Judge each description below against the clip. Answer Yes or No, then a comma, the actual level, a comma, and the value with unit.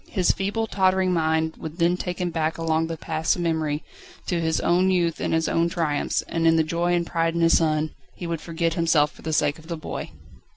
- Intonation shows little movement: Yes, narrow, 1.5 semitones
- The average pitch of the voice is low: No, medium, 165 Hz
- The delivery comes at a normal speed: No, fast, 235 wpm